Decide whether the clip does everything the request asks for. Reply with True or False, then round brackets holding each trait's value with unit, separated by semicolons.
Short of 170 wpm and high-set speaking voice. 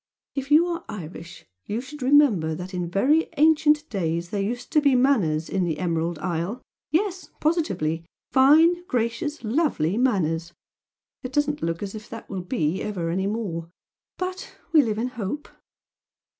True (155 wpm; 225 Hz)